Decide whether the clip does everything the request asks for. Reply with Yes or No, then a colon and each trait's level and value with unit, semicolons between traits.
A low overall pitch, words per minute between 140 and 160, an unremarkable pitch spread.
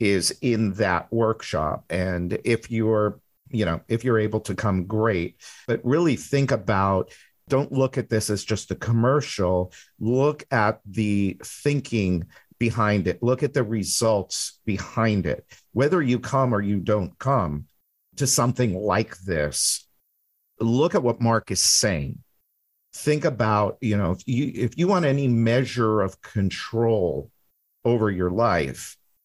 Yes: low, 110 Hz; average, 150 wpm; average, 4.1 semitones